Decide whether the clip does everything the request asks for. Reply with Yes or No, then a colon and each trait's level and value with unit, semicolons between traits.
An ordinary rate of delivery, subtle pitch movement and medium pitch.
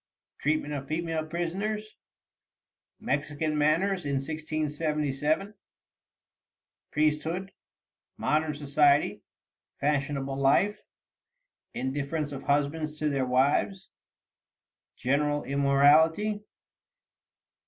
No: slow, 70 wpm; narrow, 2.3 semitones; medium, 150 Hz